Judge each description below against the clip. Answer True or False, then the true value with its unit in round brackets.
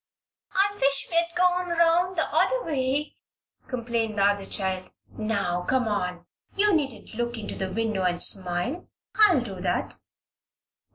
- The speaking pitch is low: False (235 Hz)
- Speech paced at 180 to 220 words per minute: False (140 wpm)